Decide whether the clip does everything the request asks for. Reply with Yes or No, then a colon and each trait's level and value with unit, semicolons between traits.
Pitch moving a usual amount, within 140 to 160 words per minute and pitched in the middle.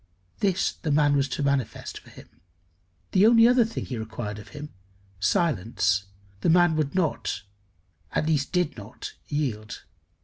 No: wide, 7.9 semitones; average, 150 wpm; medium, 145 Hz